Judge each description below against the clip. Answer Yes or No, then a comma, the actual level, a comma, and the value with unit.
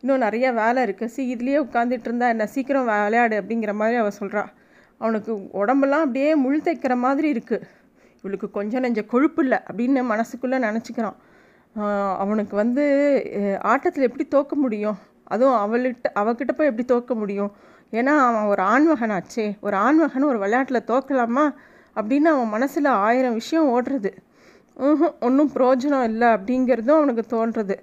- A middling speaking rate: No, fast, 140 wpm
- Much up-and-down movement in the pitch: No, average, 4.2 semitones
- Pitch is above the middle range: Yes, high, 245 Hz